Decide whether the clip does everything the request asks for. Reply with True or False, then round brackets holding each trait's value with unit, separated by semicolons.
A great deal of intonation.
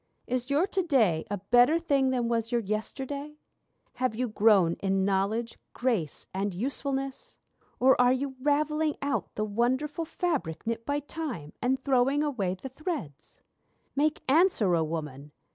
True (5.9 semitones)